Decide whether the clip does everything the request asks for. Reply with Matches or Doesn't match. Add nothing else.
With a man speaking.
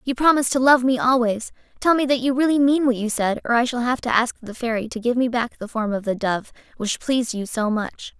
Doesn't match